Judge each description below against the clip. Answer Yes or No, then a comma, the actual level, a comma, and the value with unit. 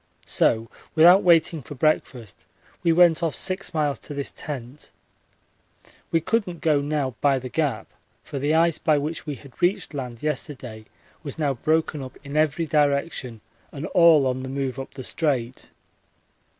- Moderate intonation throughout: Yes, average, 3.5 semitones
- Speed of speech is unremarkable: Yes, average, 165 wpm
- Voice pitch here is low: No, medium, 145 Hz